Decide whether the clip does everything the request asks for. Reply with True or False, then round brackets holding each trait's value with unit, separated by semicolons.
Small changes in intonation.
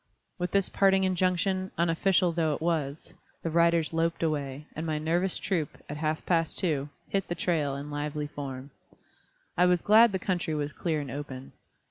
False (3.4 semitones)